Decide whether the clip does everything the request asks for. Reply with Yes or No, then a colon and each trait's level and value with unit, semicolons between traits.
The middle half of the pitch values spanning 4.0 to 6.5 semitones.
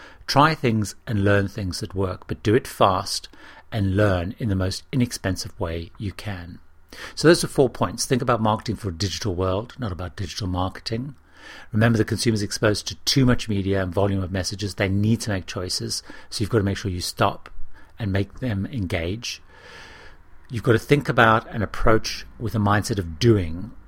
No: average, 3.5 semitones